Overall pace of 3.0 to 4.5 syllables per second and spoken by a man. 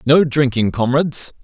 No: 4.8 syllables/s; male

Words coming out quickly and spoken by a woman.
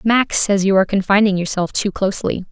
No: average, 190 wpm; female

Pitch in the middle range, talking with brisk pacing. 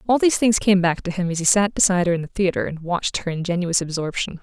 Yes: medium, 180 Hz; fast, 270 wpm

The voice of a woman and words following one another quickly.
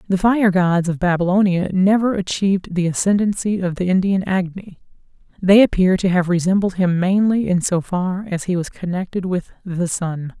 No: female; average, 175 wpm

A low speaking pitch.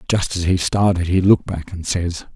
Yes: very low, 90 Hz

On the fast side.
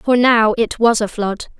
Yes: fast, 225 wpm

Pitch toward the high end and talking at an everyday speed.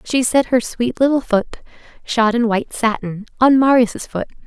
Yes: high, 235 Hz; average, 175 wpm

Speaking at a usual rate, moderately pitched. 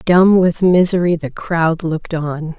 Yes: average, 165 wpm; medium, 170 Hz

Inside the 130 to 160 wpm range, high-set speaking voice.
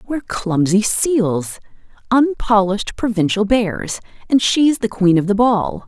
Yes: slow, 135 wpm; high, 215 Hz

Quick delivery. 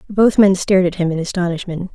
Yes: fast, 215 wpm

